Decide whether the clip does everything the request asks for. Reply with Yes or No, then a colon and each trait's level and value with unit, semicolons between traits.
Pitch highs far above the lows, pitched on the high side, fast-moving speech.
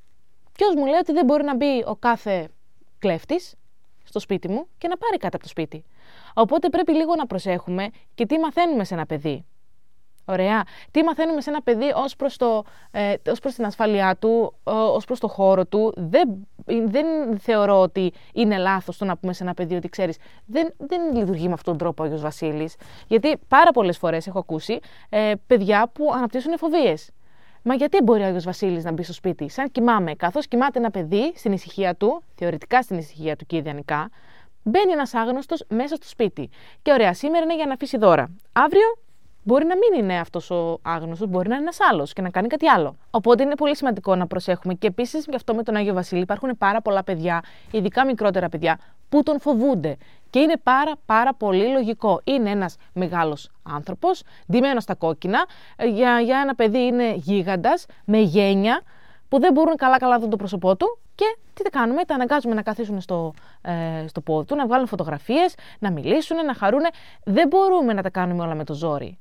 Yes: wide, 7.2 semitones; high, 220 Hz; fast, 195 wpm